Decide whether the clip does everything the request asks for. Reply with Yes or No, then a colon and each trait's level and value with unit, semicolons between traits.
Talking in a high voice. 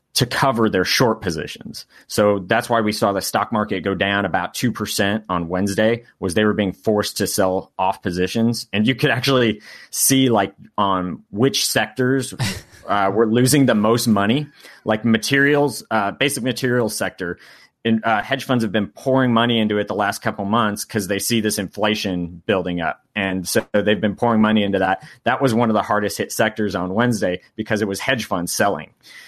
No: low, 110 Hz